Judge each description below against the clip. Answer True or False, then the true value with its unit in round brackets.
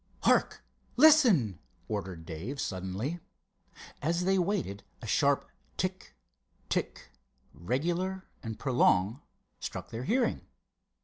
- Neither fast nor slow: False (85 wpm)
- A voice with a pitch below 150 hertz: True (135 Hz)